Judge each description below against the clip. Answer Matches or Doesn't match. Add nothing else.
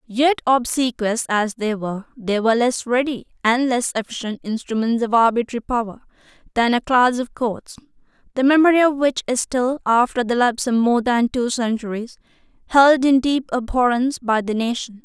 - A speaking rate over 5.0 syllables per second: Matches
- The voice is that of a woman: Matches